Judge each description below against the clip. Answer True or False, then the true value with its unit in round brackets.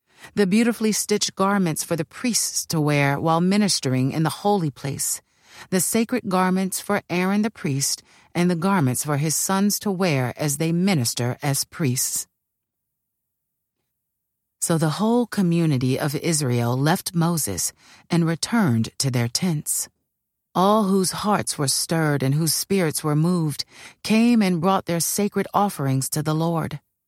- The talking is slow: False (150 wpm)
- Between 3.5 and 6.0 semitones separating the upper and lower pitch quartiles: True (5.3 semitones)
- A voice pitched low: False (165 Hz)